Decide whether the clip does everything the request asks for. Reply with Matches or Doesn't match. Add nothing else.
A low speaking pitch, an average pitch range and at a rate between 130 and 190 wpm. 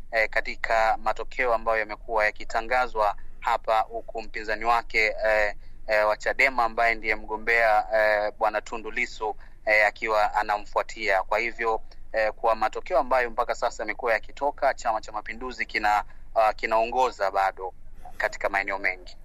Doesn't match